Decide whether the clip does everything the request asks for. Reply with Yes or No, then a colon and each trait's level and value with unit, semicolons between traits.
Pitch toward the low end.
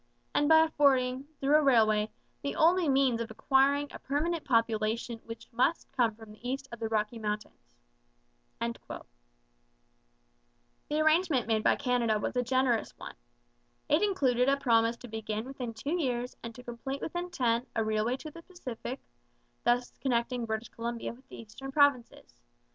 No: high, 240 Hz